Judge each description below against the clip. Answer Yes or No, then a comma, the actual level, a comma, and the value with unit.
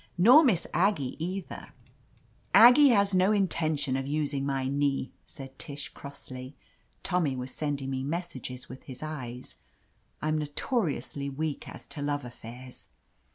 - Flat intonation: No, average, 4.7 semitones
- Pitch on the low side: No, medium, 145 Hz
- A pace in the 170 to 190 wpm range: No, average, 150 wpm